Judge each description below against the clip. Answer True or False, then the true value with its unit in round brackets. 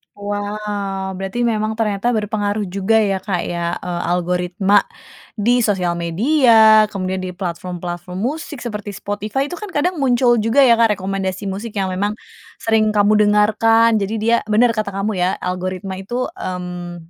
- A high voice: True (205 Hz)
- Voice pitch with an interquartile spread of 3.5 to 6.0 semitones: False (3.0 semitones)